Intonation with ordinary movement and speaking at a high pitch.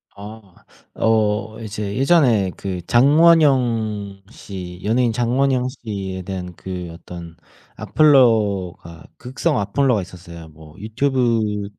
No: average, 4.9 semitones; low, 105 Hz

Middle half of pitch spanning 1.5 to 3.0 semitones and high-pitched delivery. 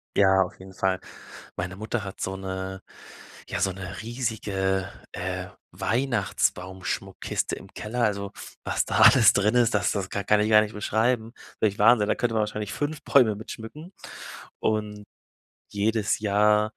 No: narrow, 2.5 semitones; low, 105 Hz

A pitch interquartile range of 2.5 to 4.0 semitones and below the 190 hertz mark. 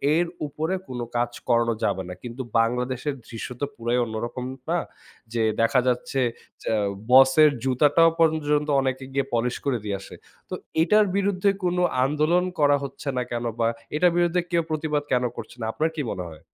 No: average, 4.7 semitones; low, 135 Hz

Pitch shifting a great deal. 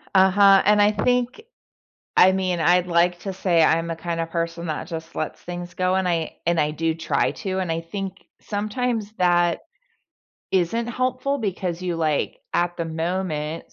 No: average, 2.9 semitones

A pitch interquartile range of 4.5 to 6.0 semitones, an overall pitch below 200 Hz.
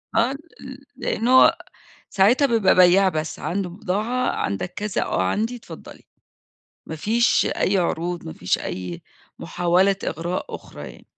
Yes: average, 5.0 semitones; high, 190 Hz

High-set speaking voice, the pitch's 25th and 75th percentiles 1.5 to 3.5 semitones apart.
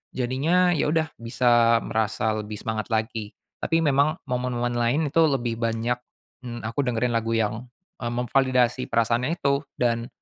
No: low, 120 Hz; average, 2.9 semitones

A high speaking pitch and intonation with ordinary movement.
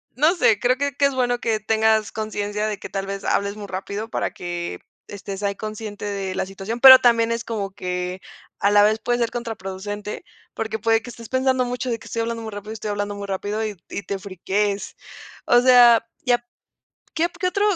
Yes: high, 215 Hz; average, 3.1 semitones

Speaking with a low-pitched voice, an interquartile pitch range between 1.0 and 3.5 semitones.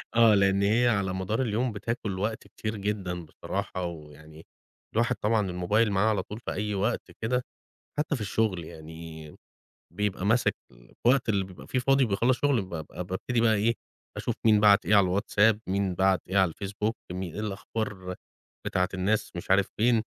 Yes: low, 100 Hz; average, 3.1 semitones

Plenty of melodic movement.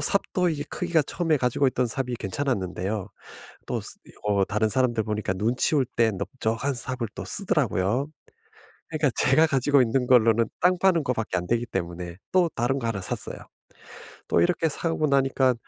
No: average, 4.9 semitones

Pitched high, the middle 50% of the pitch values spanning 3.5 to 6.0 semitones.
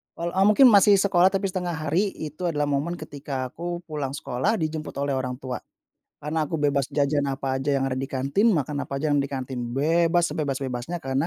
No: medium, 150 Hz; average, 4.2 semitones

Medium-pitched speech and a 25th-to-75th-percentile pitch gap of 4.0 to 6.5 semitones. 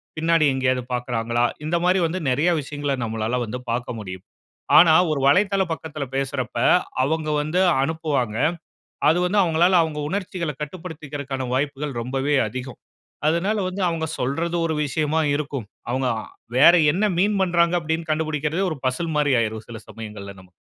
Yes: medium, 150 Hz; average, 4.6 semitones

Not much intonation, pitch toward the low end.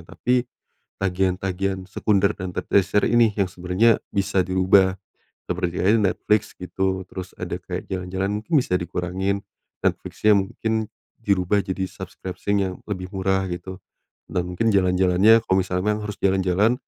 Yes: narrow, 1.9 semitones; very low, 95 Hz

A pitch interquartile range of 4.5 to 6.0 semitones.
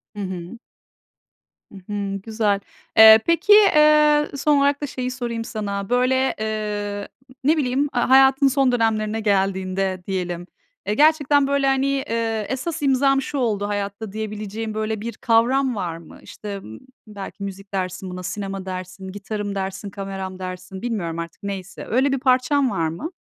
Yes: average, 5.2 semitones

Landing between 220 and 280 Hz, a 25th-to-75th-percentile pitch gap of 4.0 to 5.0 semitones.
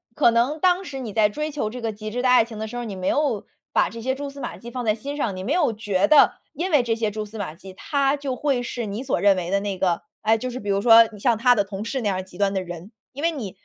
Yes: high, 225 Hz; average, 4.5 semitones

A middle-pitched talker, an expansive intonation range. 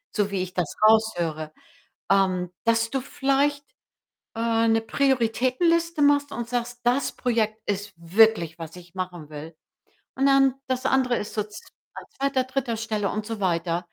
No: high, 225 Hz; wide, 5.9 semitones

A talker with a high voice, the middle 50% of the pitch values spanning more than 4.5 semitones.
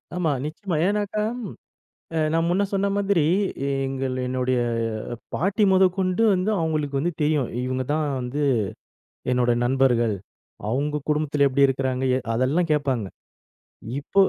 No: medium, 150 Hz; wide, 5.6 semitones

